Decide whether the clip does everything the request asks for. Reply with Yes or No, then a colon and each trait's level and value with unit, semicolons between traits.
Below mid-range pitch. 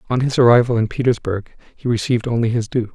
Yes: low, 120 Hz